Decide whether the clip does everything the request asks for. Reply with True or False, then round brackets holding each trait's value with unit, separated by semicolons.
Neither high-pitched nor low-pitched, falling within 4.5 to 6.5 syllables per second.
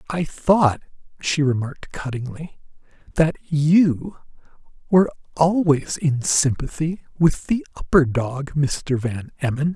False (150 Hz; 3.9 syllables/s)